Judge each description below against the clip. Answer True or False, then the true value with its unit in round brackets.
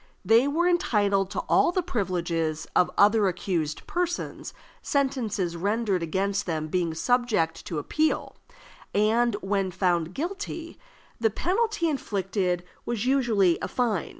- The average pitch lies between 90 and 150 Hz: False (205 Hz)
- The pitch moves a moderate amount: False (6.4 semitones)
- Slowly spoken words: True (125 wpm)